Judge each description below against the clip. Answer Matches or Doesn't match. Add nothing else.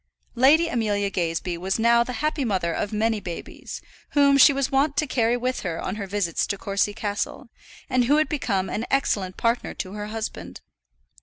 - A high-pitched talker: Matches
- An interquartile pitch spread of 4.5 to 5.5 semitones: Matches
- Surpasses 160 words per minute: Matches